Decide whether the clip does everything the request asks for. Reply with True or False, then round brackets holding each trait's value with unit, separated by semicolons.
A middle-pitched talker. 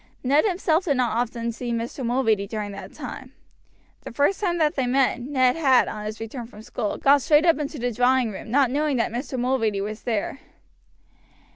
False (250 Hz)